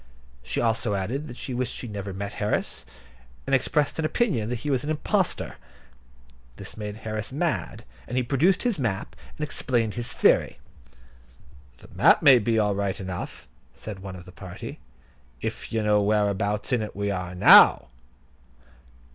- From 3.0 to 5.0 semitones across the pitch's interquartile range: Yes, average, 4.1 semitones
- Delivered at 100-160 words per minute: No, average, 170 wpm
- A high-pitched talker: No, low, 110 Hz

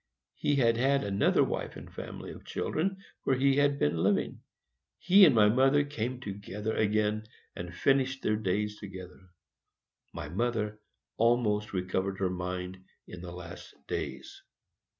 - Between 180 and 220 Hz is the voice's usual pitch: No, low, 105 Hz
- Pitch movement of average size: No, wide, 5.7 semitones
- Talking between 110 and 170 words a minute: Yes, average, 145 wpm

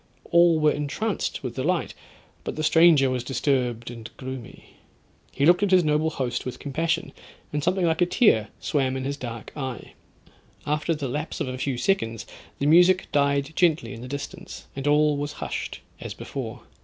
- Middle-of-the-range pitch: Yes, medium, 145 Hz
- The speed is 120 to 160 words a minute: No, average, 180 wpm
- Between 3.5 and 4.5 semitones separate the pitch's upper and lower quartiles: Yes, average, 4.0 semitones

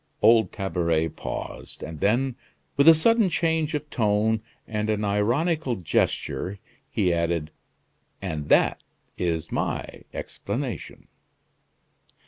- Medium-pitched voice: No, low, 105 Hz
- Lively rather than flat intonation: Yes, wide, 8.5 semitones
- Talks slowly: Yes, slow, 110 wpm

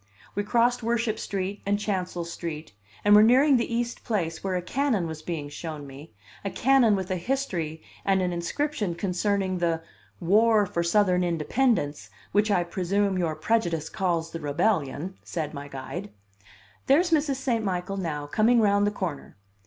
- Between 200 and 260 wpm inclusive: No, average, 165 wpm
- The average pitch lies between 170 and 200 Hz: Yes, high, 190 Hz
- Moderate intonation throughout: Yes, average, 4.9 semitones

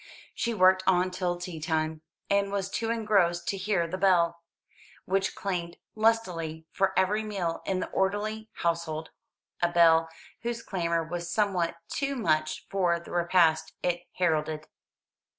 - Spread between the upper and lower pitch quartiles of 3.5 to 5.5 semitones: No, average, 2.9 semitones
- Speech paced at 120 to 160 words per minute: Yes, average, 145 wpm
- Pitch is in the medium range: Yes, medium, 180 Hz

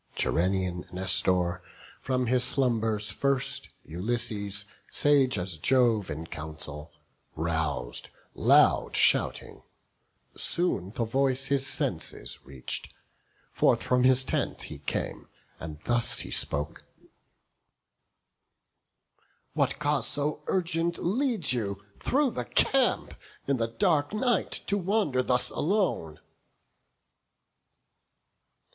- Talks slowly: Yes, slow, 100 wpm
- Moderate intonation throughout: No, wide, 8.0 semitones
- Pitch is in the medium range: No, low, 120 Hz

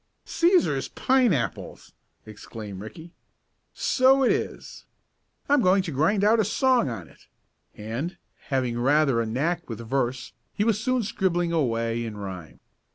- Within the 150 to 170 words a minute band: No, average, 140 wpm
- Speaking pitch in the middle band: Yes, medium, 155 Hz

